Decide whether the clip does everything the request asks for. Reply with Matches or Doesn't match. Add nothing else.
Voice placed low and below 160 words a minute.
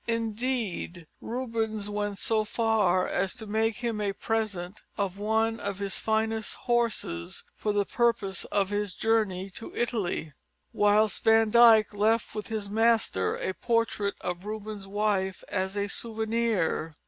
Doesn't match